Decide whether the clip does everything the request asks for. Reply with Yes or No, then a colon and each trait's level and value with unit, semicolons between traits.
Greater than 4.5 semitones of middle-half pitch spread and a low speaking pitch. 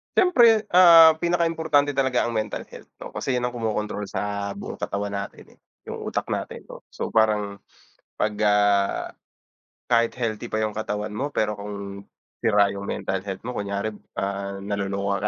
No: average, 3.7 semitones; low, 105 Hz